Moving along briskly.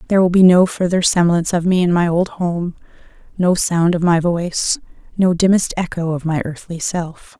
No: average, 195 wpm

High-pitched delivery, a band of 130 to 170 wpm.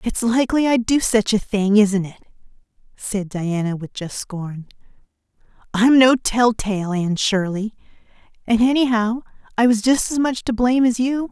Yes: high, 220 Hz; average, 160 wpm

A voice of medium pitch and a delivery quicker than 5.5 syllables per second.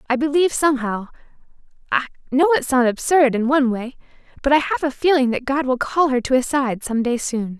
No: very high, 265 Hz; 6.0 syllables/s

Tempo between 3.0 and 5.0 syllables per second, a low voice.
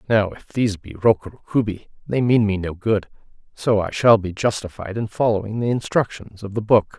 No: 5.4 syllables/s; low, 105 Hz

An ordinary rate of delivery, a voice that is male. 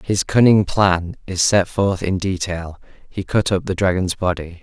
Yes: average, 180 wpm; male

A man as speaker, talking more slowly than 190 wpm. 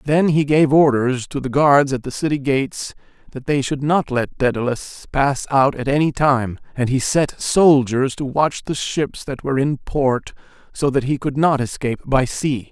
No: male; average, 200 wpm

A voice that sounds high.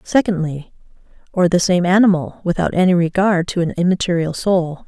No: medium, 175 Hz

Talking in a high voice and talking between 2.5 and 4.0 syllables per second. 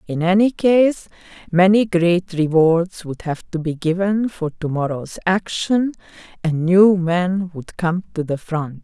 No: medium, 175 Hz; 3.8 syllables/s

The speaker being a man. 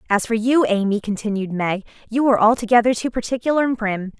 No: female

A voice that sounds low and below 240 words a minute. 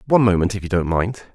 No: low, 100 Hz; fast, 270 wpm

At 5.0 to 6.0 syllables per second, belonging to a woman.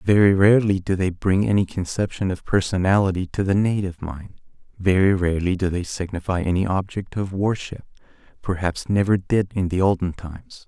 No: 5.5 syllables/s; male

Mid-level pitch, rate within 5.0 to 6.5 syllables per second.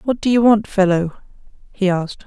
No: high, 200 Hz; 5.5 syllables/s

